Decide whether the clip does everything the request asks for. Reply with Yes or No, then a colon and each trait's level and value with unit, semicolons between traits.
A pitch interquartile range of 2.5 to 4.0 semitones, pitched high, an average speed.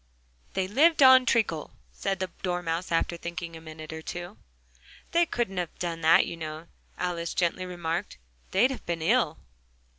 No: average, 2.9 semitones; medium, 175 Hz; average, 160 wpm